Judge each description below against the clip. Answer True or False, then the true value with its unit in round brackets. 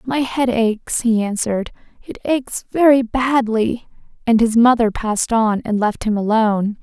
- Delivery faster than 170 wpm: False (160 wpm)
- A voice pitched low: False (230 Hz)